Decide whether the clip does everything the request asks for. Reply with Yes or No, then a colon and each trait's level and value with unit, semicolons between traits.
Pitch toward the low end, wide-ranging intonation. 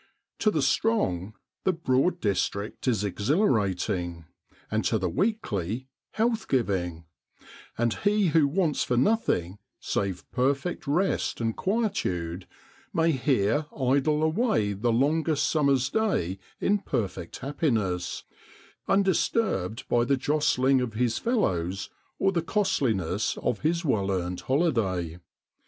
Yes: low, 130 Hz; wide, 8.9 semitones